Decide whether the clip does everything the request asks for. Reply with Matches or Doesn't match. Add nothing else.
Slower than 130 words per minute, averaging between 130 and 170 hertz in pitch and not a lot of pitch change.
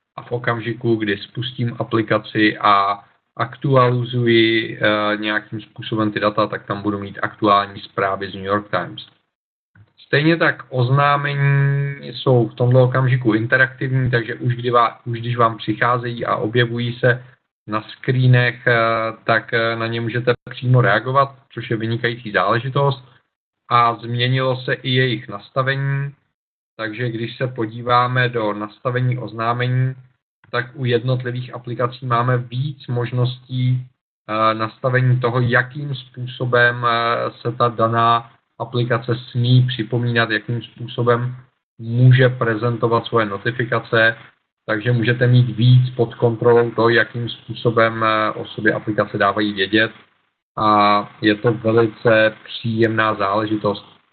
Doesn't match